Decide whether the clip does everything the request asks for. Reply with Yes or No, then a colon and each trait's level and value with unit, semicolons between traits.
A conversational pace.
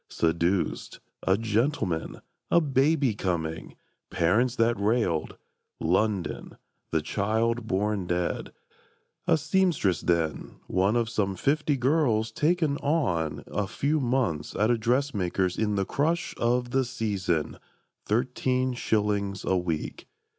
No: slow, 120 wpm